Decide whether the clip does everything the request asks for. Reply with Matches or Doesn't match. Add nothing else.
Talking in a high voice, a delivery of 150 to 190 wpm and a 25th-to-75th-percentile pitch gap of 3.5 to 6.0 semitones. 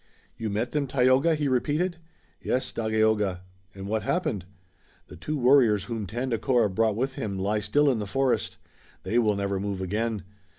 Doesn't match